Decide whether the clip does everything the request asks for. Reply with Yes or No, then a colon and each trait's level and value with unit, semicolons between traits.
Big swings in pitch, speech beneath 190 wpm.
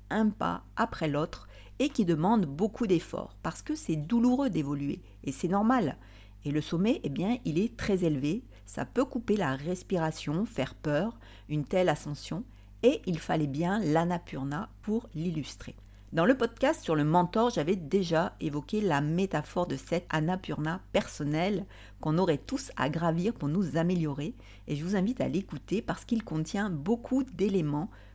Yes: wide, 5.7 semitones; average, 165 wpm